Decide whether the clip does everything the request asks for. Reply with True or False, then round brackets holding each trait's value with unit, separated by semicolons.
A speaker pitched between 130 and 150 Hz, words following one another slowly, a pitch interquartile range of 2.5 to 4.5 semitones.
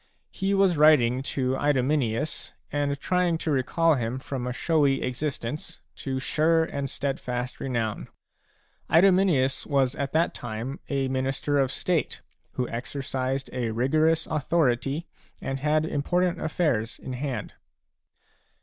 True (140 Hz; 130 wpm; 3.5 semitones)